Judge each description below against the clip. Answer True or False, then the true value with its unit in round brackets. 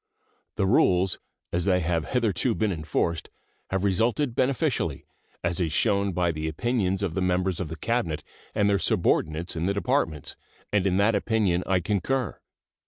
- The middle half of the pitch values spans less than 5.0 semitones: True (3.6 semitones)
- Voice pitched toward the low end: True (95 Hz)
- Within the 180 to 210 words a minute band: False (165 wpm)